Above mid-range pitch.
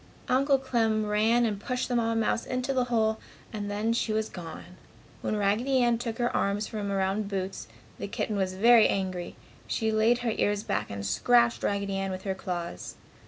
Yes: high, 215 Hz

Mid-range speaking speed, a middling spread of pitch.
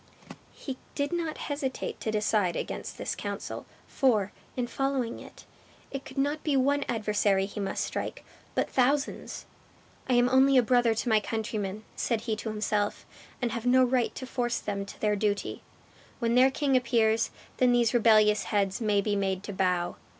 Yes: average, 175 wpm; average, 3.7 semitones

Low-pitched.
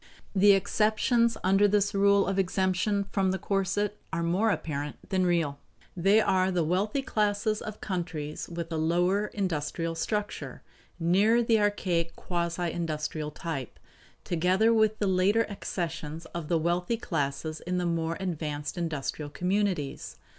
No: medium, 185 Hz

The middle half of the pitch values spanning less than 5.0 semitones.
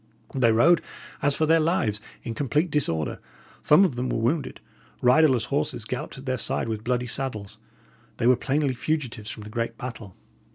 Yes: average, 4.4 semitones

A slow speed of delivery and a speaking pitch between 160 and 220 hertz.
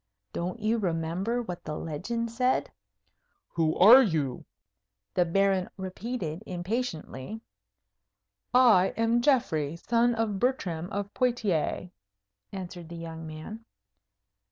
Yes: slow, 110 wpm; high, 190 Hz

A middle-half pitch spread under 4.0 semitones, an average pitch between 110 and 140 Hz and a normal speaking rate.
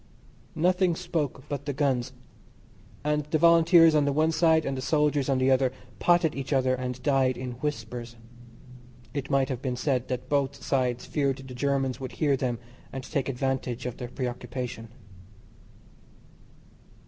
Yes: average, 2.7 semitones; low, 135 Hz; average, 160 wpm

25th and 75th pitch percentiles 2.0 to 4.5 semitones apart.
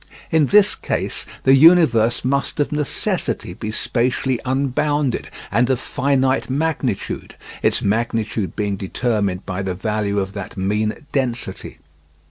No: average, 4.9 semitones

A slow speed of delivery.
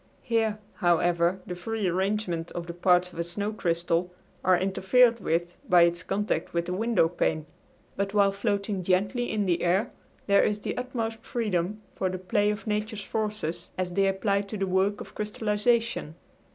No: average, 175 wpm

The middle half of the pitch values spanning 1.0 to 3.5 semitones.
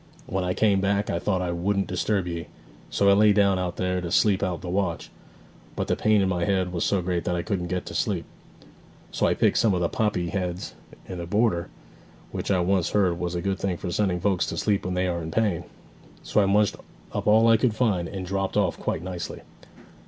Yes: narrow, 2.4 semitones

